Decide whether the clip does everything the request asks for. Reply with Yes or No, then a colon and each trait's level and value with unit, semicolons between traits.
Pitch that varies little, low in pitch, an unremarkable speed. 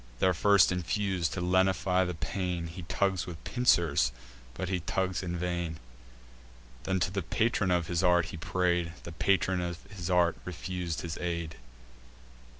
Yes: narrow, 1.6 semitones; very low, 90 Hz; average, 155 wpm